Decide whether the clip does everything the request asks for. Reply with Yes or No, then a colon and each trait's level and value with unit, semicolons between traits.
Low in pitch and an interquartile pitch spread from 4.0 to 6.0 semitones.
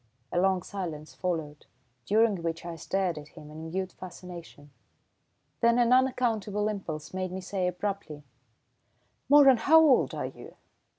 No: medium, 185 Hz; average, 4.4 semitones